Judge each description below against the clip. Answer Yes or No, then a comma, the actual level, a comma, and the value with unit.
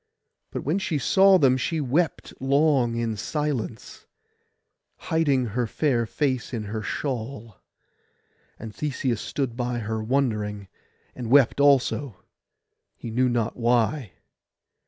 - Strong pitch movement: No, average, 3.9 semitones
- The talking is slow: Yes, slow, 120 wpm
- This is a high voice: No, low, 125 Hz